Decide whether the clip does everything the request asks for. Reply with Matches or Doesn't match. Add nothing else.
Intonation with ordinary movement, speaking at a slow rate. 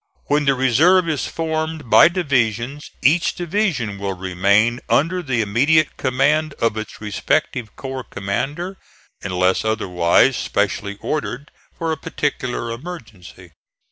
Doesn't match